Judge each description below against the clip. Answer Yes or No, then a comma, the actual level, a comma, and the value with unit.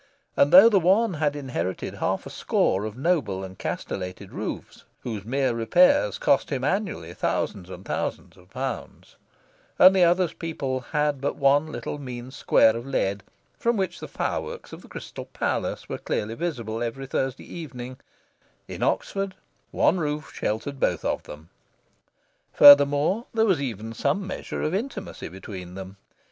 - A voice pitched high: No, low, 135 Hz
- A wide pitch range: Yes, wide, 7.6 semitones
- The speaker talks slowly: No, average, 155 wpm